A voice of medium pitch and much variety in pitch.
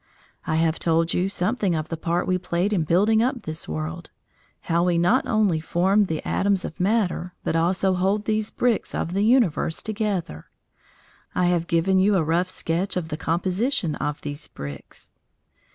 No: medium, 180 Hz; average, 3.7 semitones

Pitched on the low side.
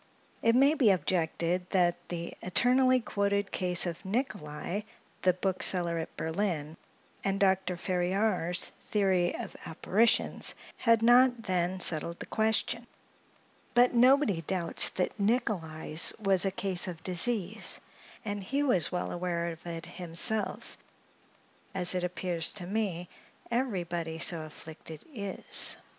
No: medium, 185 Hz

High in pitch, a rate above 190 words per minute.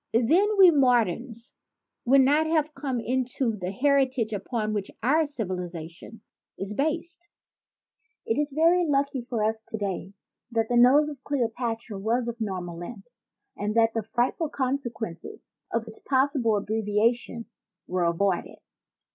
No: high, 235 Hz; average, 140 wpm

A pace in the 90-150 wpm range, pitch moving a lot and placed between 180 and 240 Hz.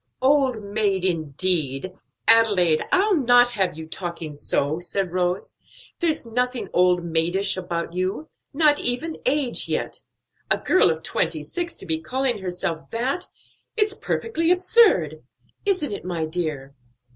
Yes: slow, 135 wpm; wide, 7.6 semitones; high, 190 Hz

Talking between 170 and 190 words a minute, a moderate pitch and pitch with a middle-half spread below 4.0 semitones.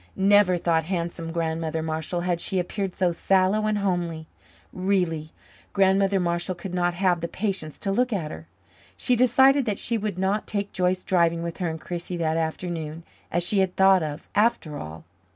Yes: average, 180 wpm; medium, 180 Hz; average, 2.9 semitones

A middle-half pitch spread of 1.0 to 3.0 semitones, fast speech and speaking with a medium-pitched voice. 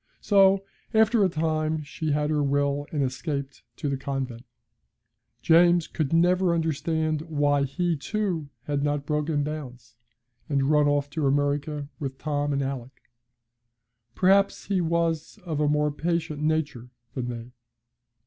No: average, 2.7 semitones; average, 140 wpm; medium, 150 Hz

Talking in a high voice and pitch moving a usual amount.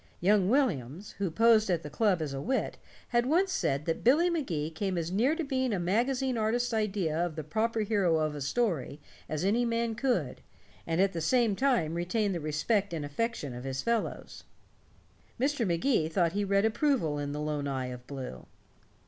No: high, 195 Hz; wide, 7.1 semitones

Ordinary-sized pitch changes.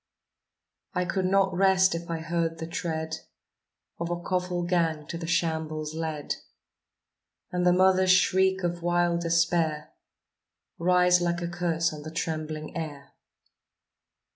No: narrow, 1.9 semitones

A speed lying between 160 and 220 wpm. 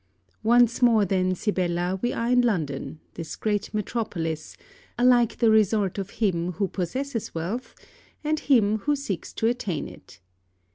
No: average, 145 wpm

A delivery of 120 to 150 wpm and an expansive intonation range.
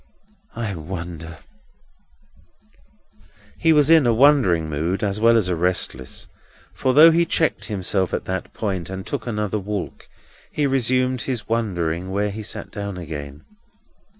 Yes: average, 145 wpm; wide, 5.8 semitones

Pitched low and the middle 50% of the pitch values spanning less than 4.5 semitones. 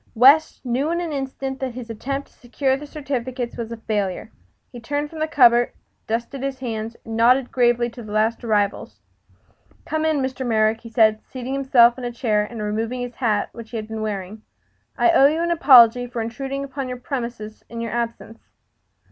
No: high, 240 Hz; average, 3.2 semitones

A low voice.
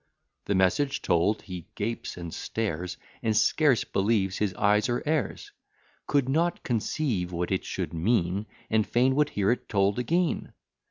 Yes: low, 105 Hz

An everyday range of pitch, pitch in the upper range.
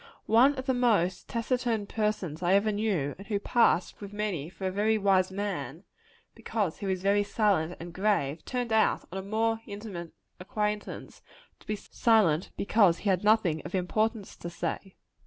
Yes: average, 3.2 semitones; high, 205 Hz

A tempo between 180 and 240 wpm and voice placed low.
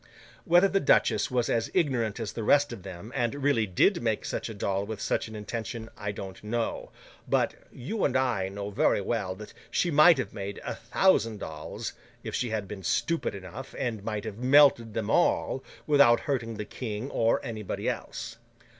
Yes: average, 190 wpm; low, 115 Hz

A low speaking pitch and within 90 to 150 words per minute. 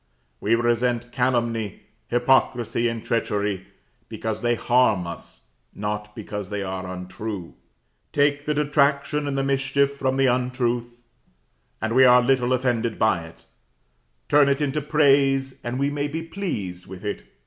Yes: low, 120 Hz; average, 145 wpm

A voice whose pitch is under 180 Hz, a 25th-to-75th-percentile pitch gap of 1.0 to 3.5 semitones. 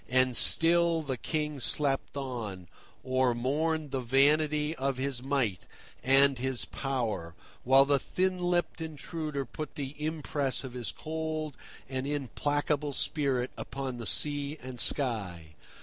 Yes: medium, 140 Hz; average, 2.8 semitones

